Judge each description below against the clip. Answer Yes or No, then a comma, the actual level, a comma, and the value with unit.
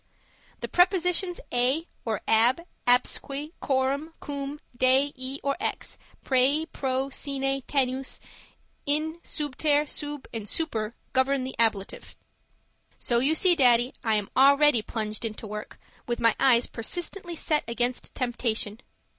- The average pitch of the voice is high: Yes, very high, 265 Hz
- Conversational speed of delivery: No, slow, 130 wpm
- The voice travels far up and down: No, average, 3.7 semitones